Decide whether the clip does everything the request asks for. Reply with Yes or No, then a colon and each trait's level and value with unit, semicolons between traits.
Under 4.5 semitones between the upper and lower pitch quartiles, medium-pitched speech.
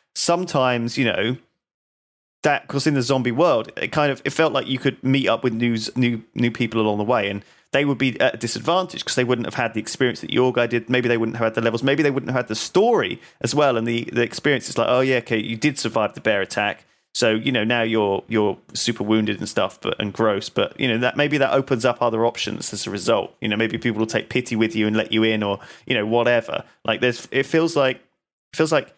No: average, 2.8 semitones; low, 120 Hz